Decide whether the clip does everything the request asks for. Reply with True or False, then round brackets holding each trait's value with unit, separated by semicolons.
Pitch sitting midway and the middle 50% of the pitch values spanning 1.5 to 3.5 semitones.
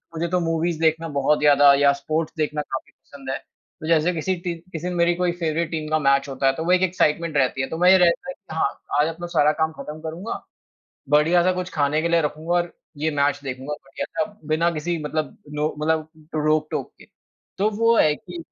True (160 Hz; 2.6 semitones)